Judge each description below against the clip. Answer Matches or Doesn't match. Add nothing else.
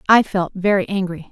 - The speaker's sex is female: Matches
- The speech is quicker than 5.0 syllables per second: Matches